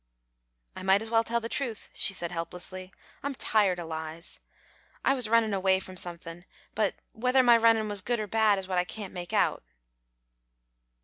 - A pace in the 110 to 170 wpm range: No, average, 185 wpm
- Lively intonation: No, average, 4.2 semitones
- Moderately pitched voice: No, high, 200 Hz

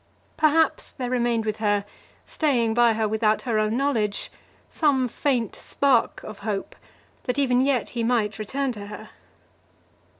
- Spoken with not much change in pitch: No, average, 3.6 semitones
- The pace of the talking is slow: No, average, 145 wpm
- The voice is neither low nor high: No, high, 235 Hz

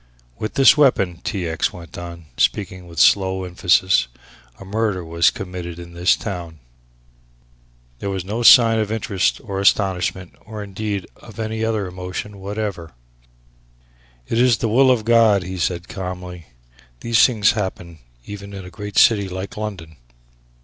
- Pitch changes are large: No, average, 3.3 semitones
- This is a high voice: No, very low, 95 Hz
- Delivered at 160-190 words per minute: No, average, 150 wpm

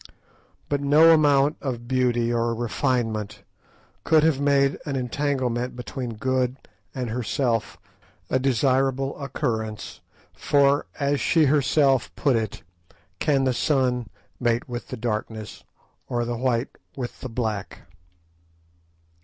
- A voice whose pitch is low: Yes, low, 130 Hz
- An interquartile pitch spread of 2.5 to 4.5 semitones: Yes, average, 2.8 semitones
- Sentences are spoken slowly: Yes, slow, 120 wpm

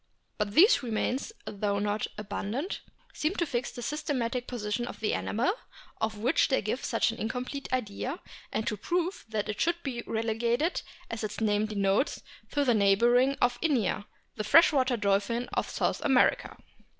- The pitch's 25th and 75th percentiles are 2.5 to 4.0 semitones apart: No, average, 4.4 semitones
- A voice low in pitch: No, high, 235 Hz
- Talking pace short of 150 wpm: No, average, 165 wpm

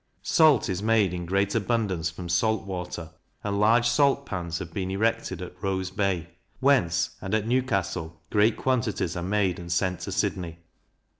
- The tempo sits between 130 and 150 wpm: No, average, 165 wpm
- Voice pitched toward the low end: Yes, very low, 95 Hz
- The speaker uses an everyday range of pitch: Yes, average, 4.0 semitones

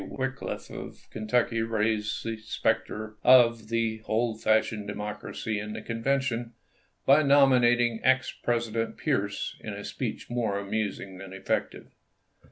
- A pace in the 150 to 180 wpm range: No, slow, 135 wpm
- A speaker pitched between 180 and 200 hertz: No, low, 115 Hz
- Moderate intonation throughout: No, narrow, 2.1 semitones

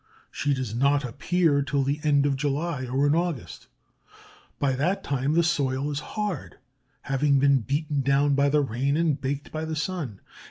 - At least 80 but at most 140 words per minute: No, average, 175 wpm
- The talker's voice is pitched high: No, medium, 140 Hz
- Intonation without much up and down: Yes, narrow, 1.9 semitones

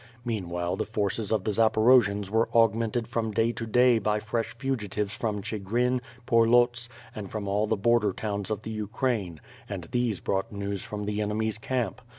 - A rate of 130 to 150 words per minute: No, average, 170 wpm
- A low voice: Yes, low, 110 Hz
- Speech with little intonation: Yes, narrow, 2.3 semitones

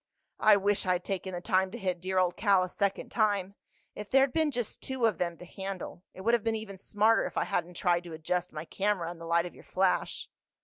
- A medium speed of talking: No, fast, 235 wpm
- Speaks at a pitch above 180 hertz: Yes, high, 190 Hz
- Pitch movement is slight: No, average, 3.0 semitones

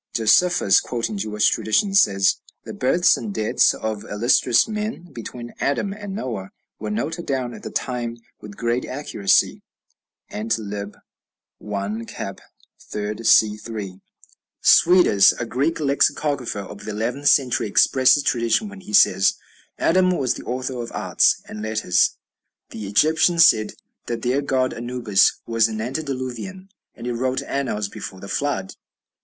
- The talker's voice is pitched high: No, low, 120 Hz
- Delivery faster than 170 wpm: No, average, 145 wpm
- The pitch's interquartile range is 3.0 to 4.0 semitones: No, average, 5.1 semitones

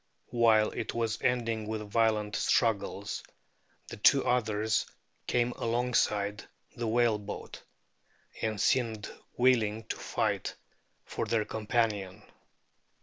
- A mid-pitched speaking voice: No, low, 110 Hz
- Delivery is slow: Yes, slow, 105 wpm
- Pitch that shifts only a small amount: Yes, narrow, 1.9 semitones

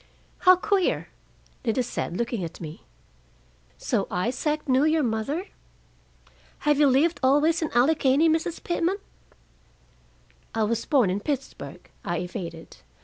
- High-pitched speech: Yes, very high, 270 Hz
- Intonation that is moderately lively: No, wide, 6.2 semitones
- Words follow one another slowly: Yes, slow, 125 wpm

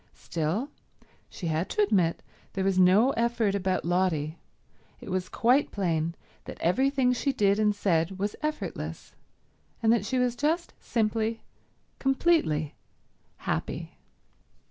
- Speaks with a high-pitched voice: Yes, high, 205 Hz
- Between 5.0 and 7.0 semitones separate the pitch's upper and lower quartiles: Yes, wide, 5.5 semitones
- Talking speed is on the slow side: Yes, slow, 125 wpm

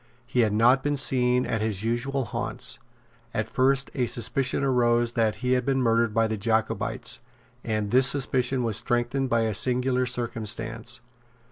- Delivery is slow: No, average, 160 wpm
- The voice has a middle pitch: No, low, 120 Hz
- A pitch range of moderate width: No, narrow, 2.3 semitones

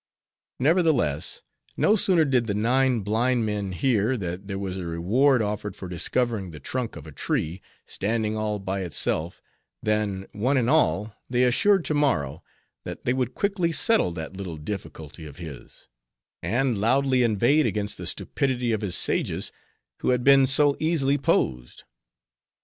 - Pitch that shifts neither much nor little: No, wide, 5.8 semitones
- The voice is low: Yes, low, 110 Hz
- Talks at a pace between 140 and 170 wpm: Yes, average, 155 wpm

